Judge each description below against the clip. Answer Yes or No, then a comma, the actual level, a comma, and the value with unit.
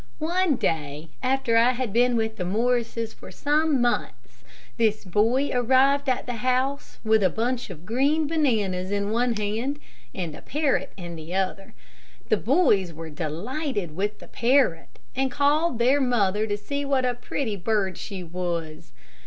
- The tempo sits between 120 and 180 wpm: Yes, average, 160 wpm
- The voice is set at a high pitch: Yes, high, 230 Hz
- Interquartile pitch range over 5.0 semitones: Yes, wide, 5.6 semitones